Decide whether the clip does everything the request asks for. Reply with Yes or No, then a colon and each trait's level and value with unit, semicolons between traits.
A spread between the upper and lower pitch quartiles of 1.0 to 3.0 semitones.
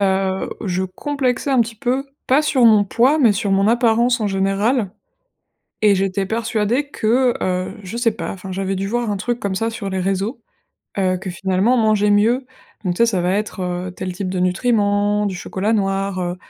No: average, 3.7 semitones